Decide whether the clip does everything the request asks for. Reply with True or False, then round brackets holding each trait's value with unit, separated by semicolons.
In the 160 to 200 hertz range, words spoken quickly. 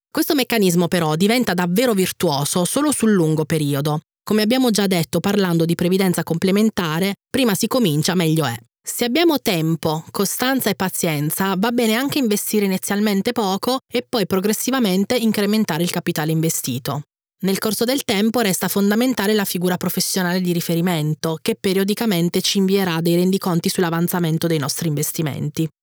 False (190 Hz; 145 wpm)